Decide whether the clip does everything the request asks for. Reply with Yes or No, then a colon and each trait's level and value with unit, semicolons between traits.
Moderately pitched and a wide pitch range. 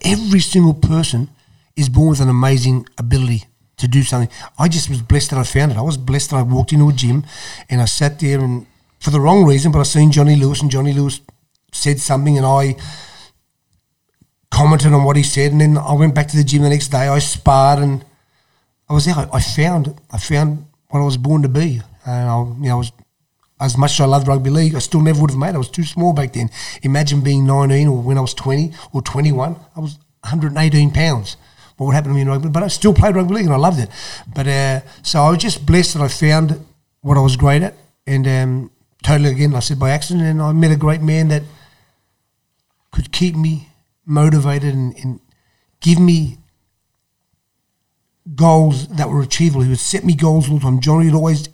No: medium, 145 Hz; narrow, 2.6 semitones